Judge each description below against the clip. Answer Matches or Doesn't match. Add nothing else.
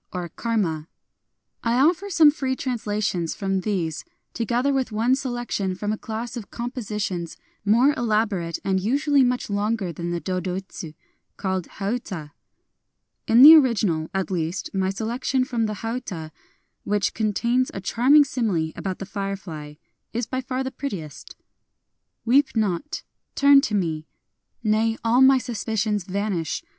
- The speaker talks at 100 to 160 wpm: Matches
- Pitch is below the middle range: Doesn't match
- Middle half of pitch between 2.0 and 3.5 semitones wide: Doesn't match